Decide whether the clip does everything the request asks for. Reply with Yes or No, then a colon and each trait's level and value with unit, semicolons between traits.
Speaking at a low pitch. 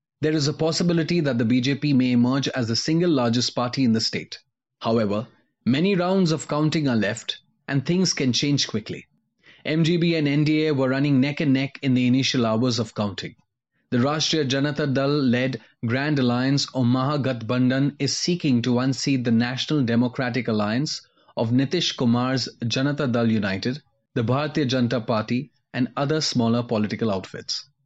Yes: low, 130 Hz